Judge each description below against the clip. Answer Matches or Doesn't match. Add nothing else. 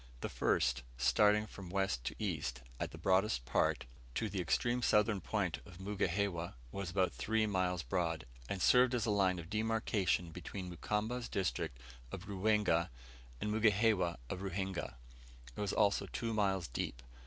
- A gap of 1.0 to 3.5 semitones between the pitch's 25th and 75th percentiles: Matches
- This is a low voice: Matches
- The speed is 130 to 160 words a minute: Matches